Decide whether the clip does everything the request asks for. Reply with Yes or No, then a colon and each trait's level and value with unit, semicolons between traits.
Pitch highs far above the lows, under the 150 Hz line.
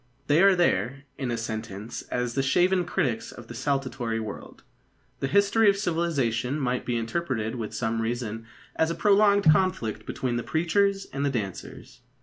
Yes: wide, 7.0 semitones; low, 135 Hz